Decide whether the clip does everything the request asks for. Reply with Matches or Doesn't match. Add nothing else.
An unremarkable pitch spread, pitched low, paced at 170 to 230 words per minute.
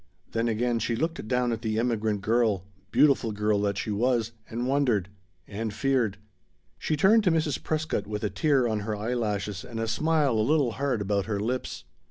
Matches